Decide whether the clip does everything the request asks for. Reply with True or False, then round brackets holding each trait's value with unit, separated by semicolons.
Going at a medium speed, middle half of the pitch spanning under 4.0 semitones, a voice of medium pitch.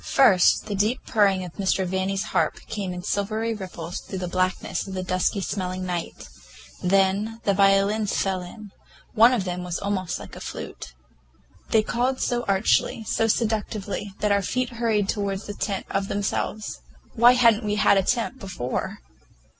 False (170 wpm; 2.6 semitones; 200 Hz)